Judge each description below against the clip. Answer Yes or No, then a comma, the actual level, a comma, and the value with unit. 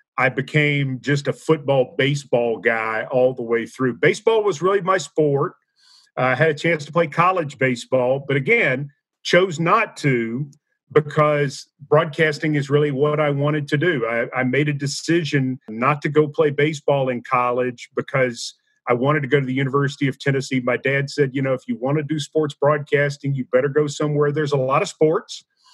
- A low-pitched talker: No, medium, 145 Hz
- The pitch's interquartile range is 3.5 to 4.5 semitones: No, average, 2.9 semitones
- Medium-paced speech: Yes, average, 190 wpm